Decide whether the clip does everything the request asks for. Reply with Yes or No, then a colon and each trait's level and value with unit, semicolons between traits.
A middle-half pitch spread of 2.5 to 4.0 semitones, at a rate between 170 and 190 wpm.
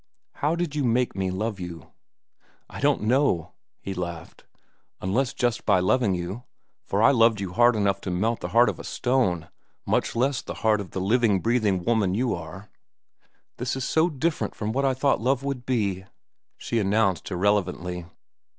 No: average, 5.0 semitones; average, 180 wpm